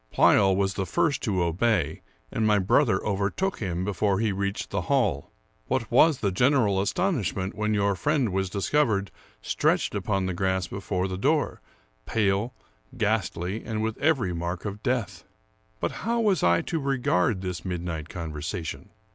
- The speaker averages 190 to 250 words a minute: No, average, 155 wpm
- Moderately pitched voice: No, low, 100 Hz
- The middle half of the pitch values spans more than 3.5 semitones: Yes, average, 4.2 semitones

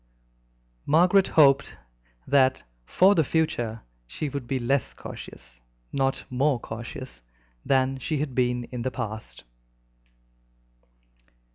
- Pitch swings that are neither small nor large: Yes, average, 3.2 semitones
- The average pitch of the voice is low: Yes, low, 130 Hz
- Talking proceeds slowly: Yes, slow, 110 wpm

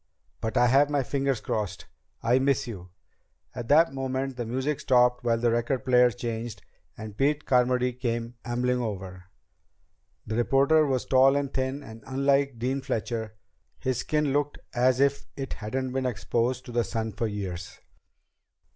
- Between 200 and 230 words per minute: No, average, 160 wpm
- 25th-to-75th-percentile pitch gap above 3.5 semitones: No, average, 2.7 semitones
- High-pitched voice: No, low, 125 Hz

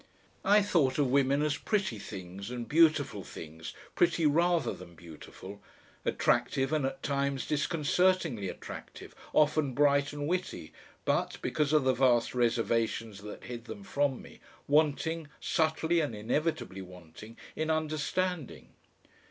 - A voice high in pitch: No, medium, 140 Hz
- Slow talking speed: Yes, slow, 130 wpm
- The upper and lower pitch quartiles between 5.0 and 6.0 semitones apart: Yes, wide, 5.5 semitones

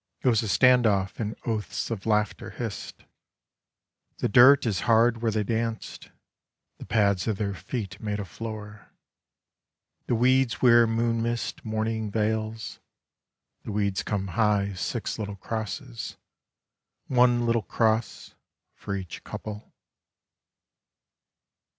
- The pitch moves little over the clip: Yes, narrow, 2.1 semitones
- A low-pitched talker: Yes, low, 110 Hz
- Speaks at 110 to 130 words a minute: Yes, slow, 125 wpm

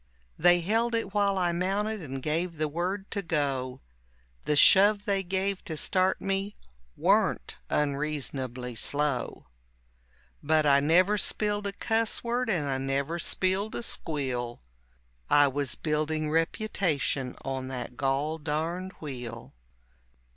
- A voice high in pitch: No, medium, 160 Hz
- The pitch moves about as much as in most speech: No, wide, 5.7 semitones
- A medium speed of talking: No, slow, 130 wpm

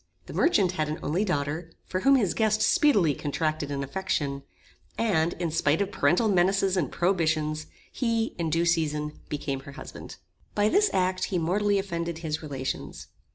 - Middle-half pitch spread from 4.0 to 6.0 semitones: Yes, average, 4.4 semitones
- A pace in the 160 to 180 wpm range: Yes, average, 165 wpm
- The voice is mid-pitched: Yes, medium, 170 Hz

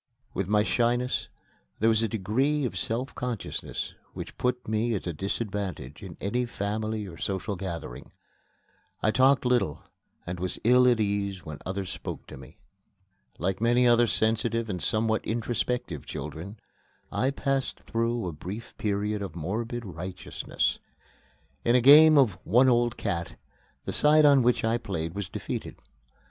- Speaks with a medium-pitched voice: No, low, 110 Hz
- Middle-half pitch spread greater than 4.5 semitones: No, average, 4.1 semitones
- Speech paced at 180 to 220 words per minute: No, average, 155 wpm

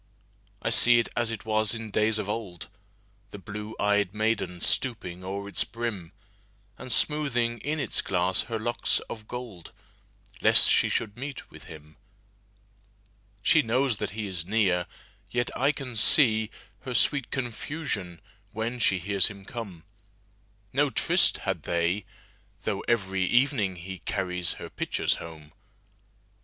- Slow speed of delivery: Yes, slow, 125 wpm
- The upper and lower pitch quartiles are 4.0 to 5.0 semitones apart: No, average, 3.6 semitones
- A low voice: Yes, low, 105 Hz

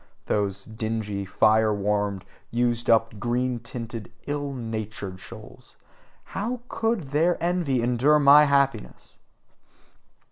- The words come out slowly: Yes, slow, 105 wpm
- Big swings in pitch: No, average, 4.7 semitones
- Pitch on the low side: Yes, low, 120 Hz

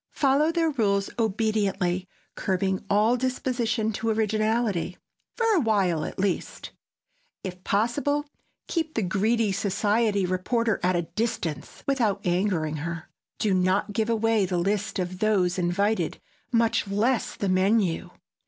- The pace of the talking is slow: Yes, slow, 125 wpm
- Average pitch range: Yes, average, 3.6 semitones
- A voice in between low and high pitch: No, high, 205 Hz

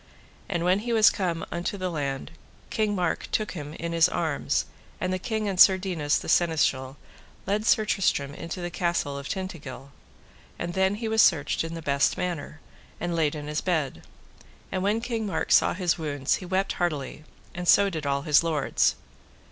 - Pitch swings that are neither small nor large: Yes, average, 4.3 semitones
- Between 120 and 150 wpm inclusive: No, average, 190 wpm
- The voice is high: No, medium, 175 Hz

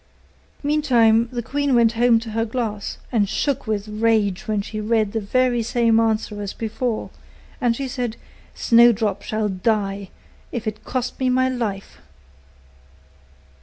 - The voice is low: No, high, 225 Hz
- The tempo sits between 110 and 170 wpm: Yes, average, 145 wpm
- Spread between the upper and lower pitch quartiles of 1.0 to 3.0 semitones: Yes, narrow, 2.4 semitones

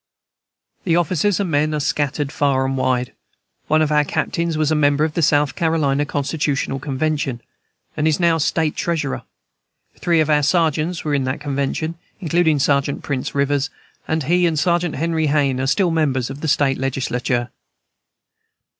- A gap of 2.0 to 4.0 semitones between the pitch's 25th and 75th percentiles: Yes, narrow, 2.6 semitones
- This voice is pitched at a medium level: Yes, medium, 150 Hz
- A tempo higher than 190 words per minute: No, average, 165 wpm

